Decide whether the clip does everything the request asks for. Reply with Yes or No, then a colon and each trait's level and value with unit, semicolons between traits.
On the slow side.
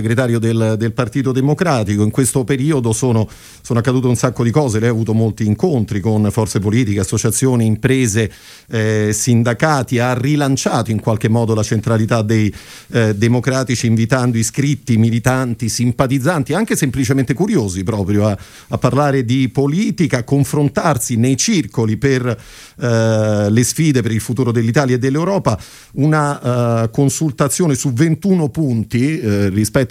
No: average, 140 wpm